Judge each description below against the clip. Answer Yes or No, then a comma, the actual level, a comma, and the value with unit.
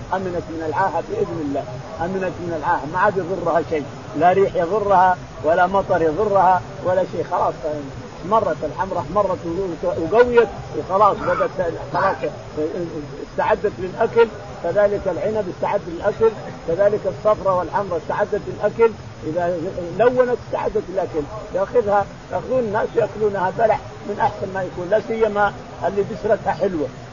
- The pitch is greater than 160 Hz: Yes, medium, 185 Hz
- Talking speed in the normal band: Yes, average, 125 wpm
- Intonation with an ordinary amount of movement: Yes, average, 4.1 semitones